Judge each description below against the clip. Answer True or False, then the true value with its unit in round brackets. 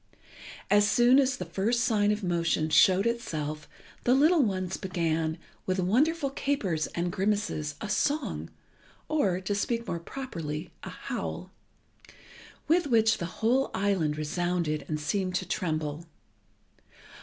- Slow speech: True (130 wpm)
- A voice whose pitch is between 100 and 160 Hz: False (190 Hz)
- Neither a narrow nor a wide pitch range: False (5.9 semitones)